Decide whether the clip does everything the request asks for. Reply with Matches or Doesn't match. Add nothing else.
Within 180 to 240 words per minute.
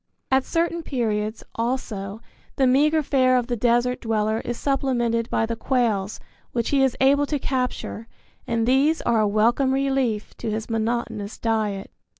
Doesn't match